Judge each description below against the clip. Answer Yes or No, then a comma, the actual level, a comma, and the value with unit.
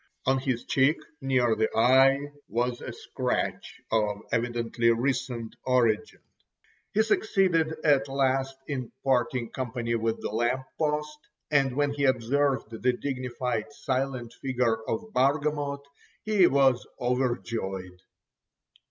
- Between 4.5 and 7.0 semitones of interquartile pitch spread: No, average, 3.1 semitones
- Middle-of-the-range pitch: No, low, 130 Hz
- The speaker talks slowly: Yes, slow, 115 wpm